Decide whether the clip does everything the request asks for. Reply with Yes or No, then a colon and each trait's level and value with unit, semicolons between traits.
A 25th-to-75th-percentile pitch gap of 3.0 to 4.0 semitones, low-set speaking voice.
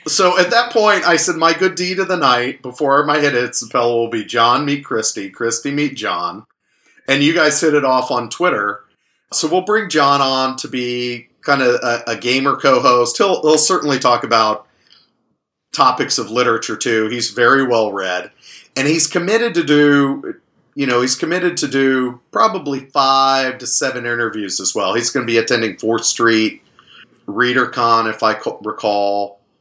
No: average, 4.6 semitones; low, 130 Hz